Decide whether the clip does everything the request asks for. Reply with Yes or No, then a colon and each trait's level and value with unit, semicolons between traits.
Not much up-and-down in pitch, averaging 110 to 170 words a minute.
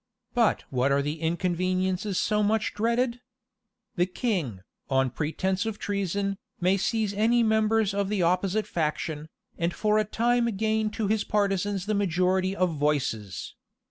No: average, 4.0 semitones; average, 145 wpm